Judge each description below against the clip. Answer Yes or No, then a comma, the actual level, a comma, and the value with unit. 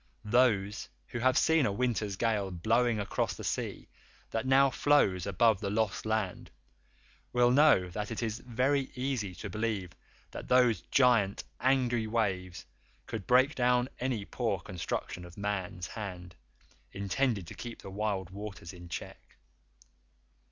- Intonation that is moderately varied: Yes, average, 4.3 semitones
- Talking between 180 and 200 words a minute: No, average, 145 wpm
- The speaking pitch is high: No, low, 110 Hz